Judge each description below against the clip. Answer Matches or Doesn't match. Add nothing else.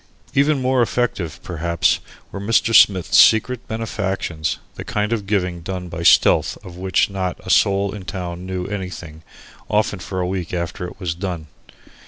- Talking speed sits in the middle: Matches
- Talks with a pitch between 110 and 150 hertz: Doesn't match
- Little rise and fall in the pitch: Doesn't match